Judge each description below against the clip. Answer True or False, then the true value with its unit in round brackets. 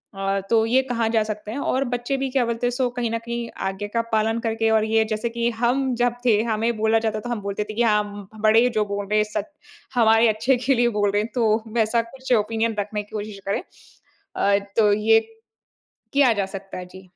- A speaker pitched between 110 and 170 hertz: False (225 Hz)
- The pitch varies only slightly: True (2.1 semitones)